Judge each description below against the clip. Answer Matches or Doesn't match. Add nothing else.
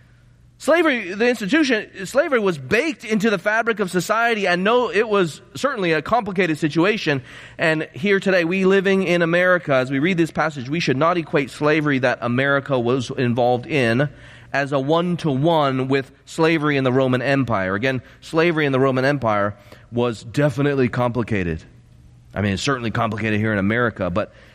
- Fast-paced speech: Doesn't match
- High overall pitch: Doesn't match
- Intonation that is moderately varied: Doesn't match